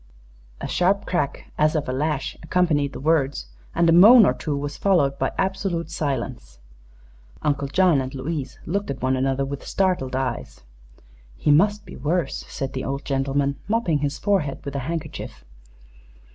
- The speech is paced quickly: No, average, 165 wpm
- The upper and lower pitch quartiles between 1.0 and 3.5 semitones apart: No, average, 4.3 semitones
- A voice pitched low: No, medium, 145 Hz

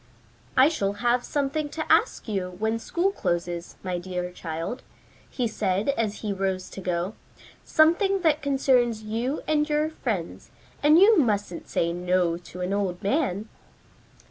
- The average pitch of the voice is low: No, high, 215 Hz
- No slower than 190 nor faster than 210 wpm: No, average, 150 wpm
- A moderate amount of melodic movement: No, wide, 7.9 semitones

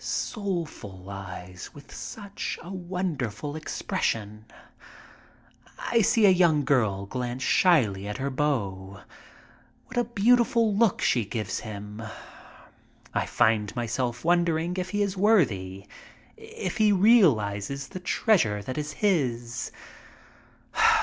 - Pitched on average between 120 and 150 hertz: Yes, medium, 140 Hz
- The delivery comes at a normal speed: No, slow, 115 wpm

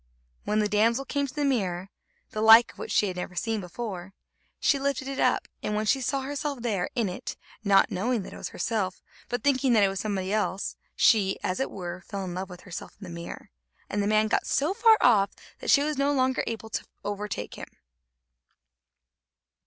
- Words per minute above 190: Yes, fast, 205 wpm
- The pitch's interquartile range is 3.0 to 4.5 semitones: No, wide, 5.4 semitones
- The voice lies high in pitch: Yes, high, 215 Hz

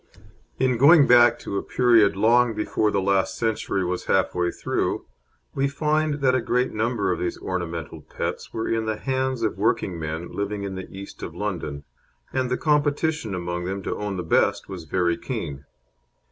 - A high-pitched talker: No, low, 105 Hz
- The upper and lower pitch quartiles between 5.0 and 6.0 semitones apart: Yes, wide, 5.5 semitones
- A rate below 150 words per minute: No, average, 190 wpm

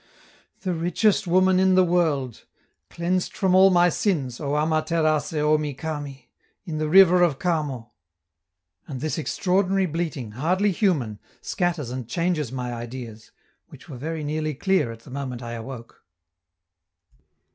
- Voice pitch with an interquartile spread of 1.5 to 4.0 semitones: No, average, 5.3 semitones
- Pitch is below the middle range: No, medium, 155 Hz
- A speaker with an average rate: Yes, average, 145 wpm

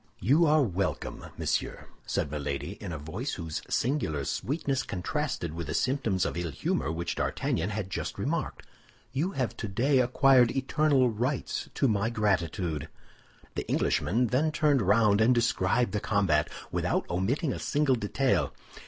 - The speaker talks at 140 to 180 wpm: Yes, average, 150 wpm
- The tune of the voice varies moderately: No, wide, 7.5 semitones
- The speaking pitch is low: Yes, low, 110 Hz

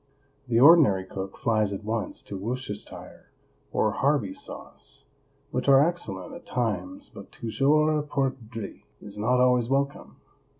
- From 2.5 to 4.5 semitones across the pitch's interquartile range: No, average, 4.9 semitones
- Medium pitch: No, low, 125 Hz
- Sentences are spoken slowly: Yes, slow, 130 wpm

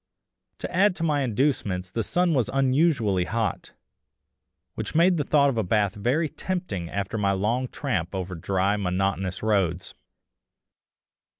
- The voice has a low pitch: Yes, low, 110 Hz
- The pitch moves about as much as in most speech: No, wide, 6.8 semitones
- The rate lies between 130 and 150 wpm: Yes, average, 140 wpm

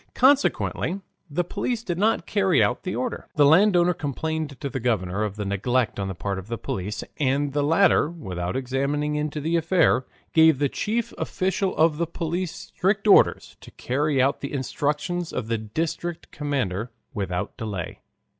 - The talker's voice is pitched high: No, medium, 145 Hz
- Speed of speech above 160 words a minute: Yes, average, 170 wpm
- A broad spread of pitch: Yes, wide, 6.2 semitones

